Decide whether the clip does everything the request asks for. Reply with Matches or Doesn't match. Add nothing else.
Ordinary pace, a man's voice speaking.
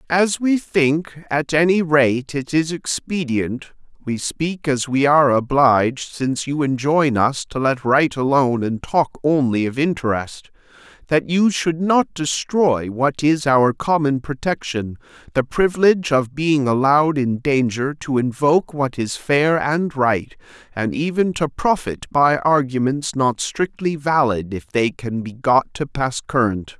Matches